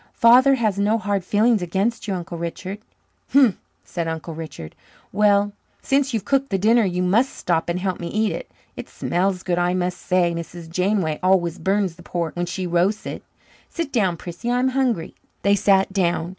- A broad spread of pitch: No, average, 3.8 semitones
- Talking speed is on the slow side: No, average, 185 wpm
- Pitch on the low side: No, high, 190 Hz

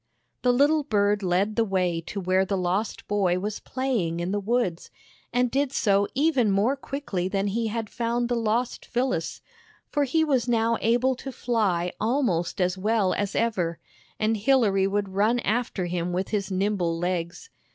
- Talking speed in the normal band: Yes, average, 170 wpm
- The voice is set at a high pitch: Yes, high, 210 Hz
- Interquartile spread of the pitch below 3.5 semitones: No, average, 4.5 semitones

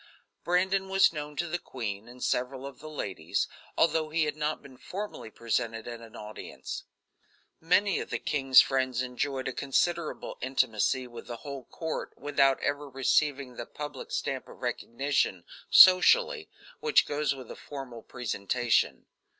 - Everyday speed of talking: Yes, average, 150 wpm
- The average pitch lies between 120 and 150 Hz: Yes, low, 135 Hz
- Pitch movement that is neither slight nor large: Yes, average, 4.0 semitones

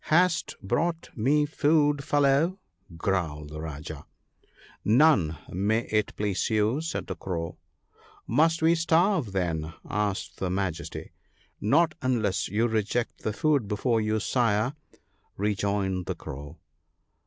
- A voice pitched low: Yes, low, 105 Hz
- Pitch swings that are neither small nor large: No, wide, 7.4 semitones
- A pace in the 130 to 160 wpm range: Yes, average, 150 wpm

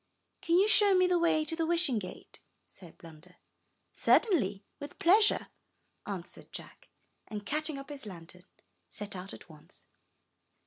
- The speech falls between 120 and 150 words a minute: Yes, average, 145 wpm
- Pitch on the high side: Yes, very high, 275 Hz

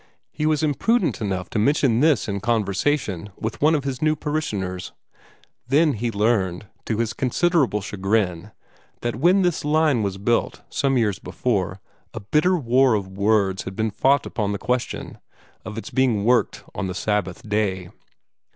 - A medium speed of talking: Yes, average, 160 wpm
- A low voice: Yes, low, 115 Hz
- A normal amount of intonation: No, wide, 6.0 semitones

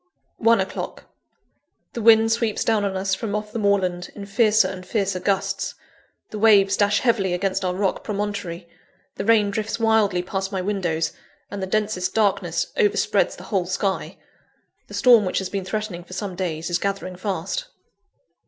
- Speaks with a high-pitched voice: Yes, high, 200 Hz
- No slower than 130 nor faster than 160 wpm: No, average, 170 wpm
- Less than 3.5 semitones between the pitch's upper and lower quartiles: Yes, narrow, 2.5 semitones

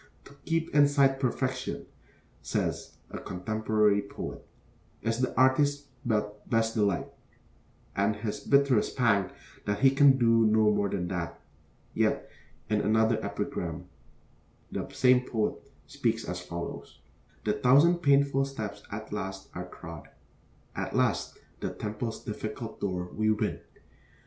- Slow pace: Yes, slow, 130 wpm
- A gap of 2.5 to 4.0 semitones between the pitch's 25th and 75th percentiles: No, average, 4.4 semitones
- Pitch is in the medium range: No, low, 110 Hz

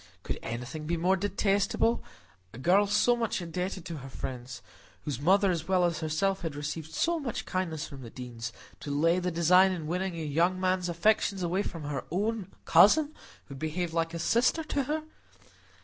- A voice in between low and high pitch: Yes, medium, 175 Hz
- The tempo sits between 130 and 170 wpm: No, average, 180 wpm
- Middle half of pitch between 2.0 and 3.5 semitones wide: No, average, 4.3 semitones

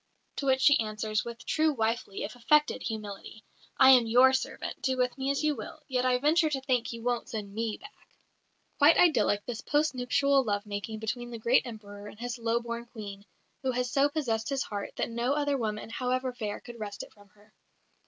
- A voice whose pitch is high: Yes, high, 240 Hz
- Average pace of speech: No, fast, 210 wpm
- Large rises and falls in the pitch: No, average, 3.5 semitones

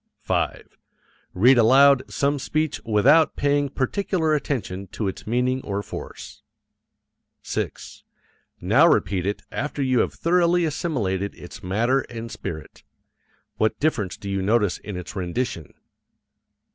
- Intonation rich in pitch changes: Yes, wide, 6.3 semitones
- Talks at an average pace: No, slow, 125 wpm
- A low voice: Yes, low, 120 Hz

